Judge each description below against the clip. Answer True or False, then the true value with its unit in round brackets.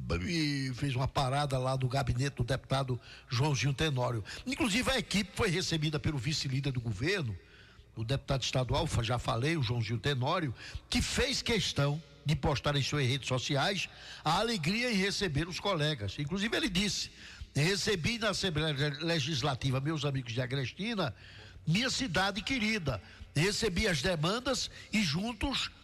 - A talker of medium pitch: True (145 Hz)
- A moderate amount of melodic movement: False (6.3 semitones)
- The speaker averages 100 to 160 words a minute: True (145 wpm)